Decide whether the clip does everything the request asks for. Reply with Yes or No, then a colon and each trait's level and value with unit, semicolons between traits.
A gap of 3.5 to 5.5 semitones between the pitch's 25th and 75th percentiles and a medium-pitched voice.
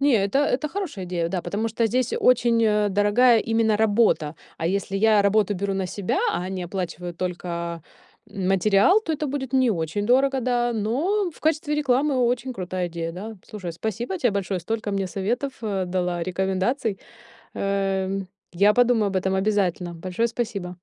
No: average, 4.6 semitones; high, 205 Hz